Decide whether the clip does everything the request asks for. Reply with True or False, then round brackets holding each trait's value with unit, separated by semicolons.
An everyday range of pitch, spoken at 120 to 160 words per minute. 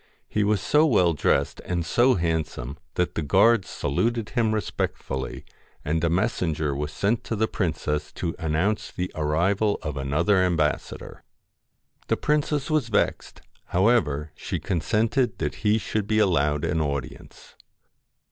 False (6.2 semitones; 140 wpm)